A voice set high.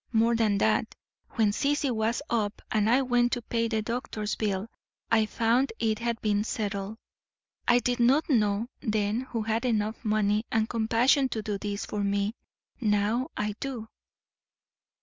Yes: high, 220 Hz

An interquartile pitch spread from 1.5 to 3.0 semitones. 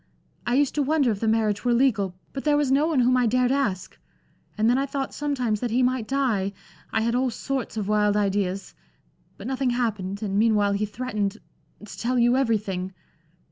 No: average, 3.9 semitones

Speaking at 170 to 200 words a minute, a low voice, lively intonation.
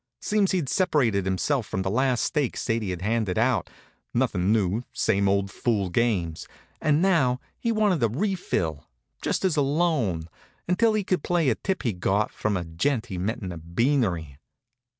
Yes: average, 175 wpm; low, 115 Hz; wide, 8.0 semitones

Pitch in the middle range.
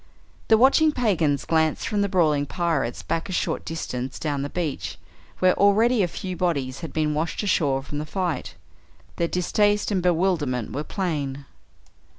Yes: medium, 165 Hz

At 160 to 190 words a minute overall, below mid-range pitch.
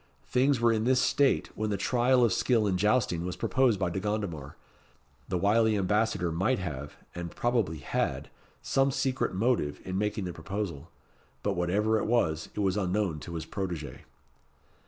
Yes: average, 170 wpm; low, 100 Hz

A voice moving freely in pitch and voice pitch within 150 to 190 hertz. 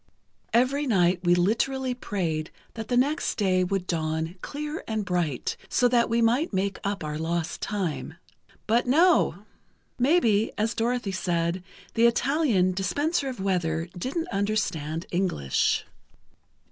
No: wide, 6.0 semitones; high, 200 Hz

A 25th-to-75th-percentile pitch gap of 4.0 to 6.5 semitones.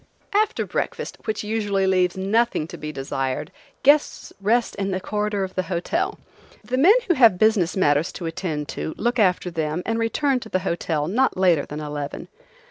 Yes: wide, 5.6 semitones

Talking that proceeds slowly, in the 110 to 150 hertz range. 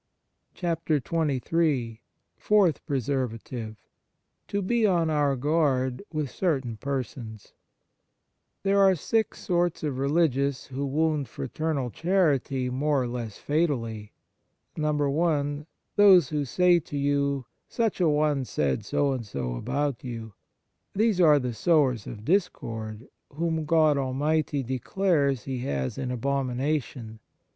Yes: slow, 120 wpm; medium, 140 Hz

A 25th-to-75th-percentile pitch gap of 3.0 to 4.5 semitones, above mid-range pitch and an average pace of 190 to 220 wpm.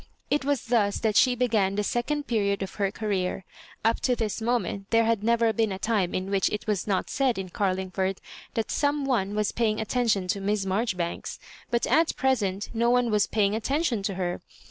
Yes: average, 3.4 semitones; high, 215 Hz; average, 200 wpm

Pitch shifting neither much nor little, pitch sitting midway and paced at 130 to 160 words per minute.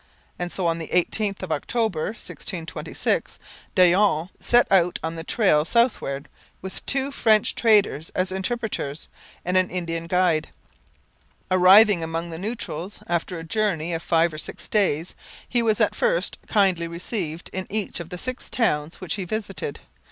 Yes: average, 4.3 semitones; medium, 180 Hz; average, 155 wpm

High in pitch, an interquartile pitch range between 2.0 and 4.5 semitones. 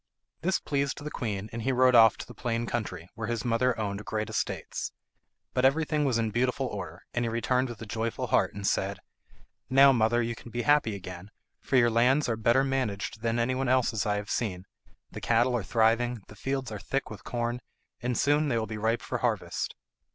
No: low, 120 Hz; average, 2.8 semitones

